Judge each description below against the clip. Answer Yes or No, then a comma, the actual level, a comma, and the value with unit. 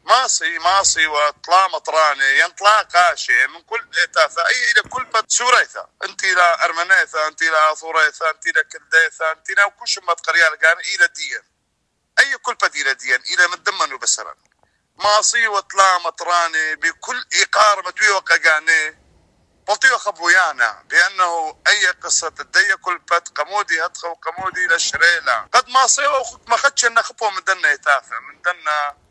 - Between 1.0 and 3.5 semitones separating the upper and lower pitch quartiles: No, average, 5.3 semitones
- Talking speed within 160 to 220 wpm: No, average, 145 wpm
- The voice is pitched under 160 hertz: No, high, 190 Hz